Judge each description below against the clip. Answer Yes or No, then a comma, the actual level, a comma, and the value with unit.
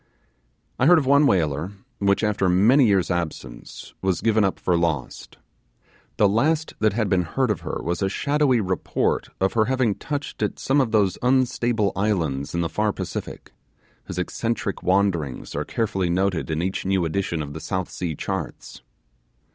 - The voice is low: Yes, low, 100 Hz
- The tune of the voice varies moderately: Yes, average, 4.7 semitones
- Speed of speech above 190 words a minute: No, average, 170 wpm